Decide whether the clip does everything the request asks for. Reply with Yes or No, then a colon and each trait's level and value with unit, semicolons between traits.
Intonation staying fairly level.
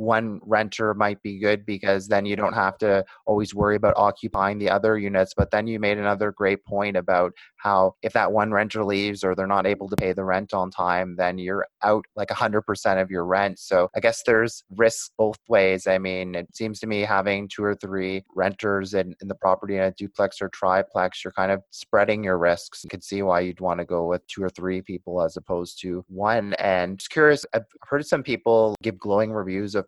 Yes: narrow, 2.1 semitones